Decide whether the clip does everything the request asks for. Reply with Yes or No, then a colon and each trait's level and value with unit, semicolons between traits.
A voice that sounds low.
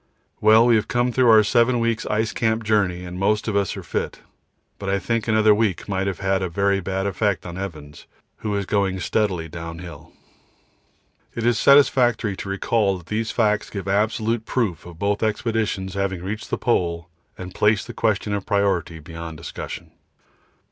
Yes: low, 100 Hz